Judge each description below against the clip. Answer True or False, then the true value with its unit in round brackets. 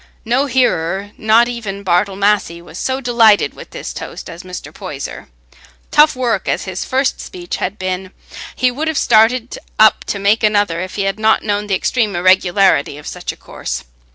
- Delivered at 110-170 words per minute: False (180 wpm)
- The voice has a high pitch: True (205 Hz)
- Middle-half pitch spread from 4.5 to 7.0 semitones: False (4.0 semitones)